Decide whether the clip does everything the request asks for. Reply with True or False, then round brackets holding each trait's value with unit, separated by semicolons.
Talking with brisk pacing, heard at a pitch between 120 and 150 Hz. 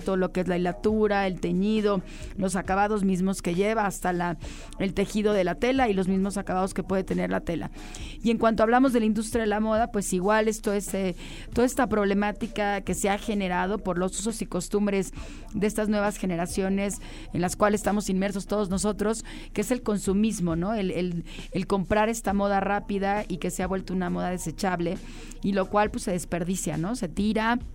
False (210 wpm; 200 Hz)